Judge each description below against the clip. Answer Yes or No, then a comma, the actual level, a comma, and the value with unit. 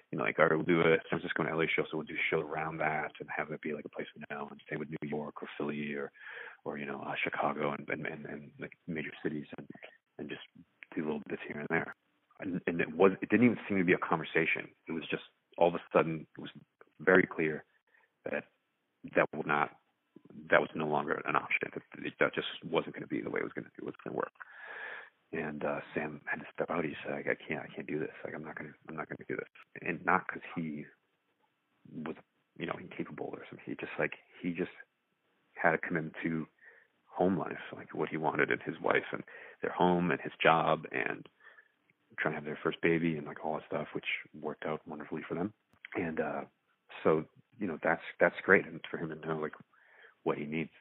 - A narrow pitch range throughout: Yes, narrow, 1.8 semitones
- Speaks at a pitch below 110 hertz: Yes, very low, 75 Hz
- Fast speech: Yes, fast, 245 wpm